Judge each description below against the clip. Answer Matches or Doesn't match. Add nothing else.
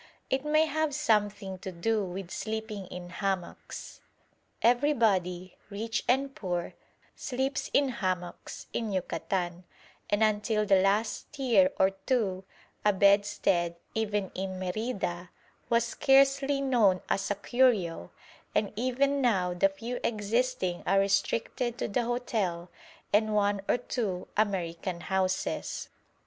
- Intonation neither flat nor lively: Matches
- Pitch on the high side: Matches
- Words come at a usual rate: Doesn't match